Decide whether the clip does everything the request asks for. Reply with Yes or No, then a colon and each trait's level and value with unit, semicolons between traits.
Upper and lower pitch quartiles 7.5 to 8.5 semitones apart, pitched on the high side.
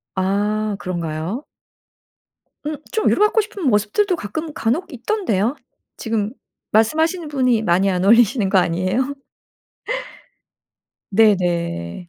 Yes: wide, 7.8 semitones; high, 220 Hz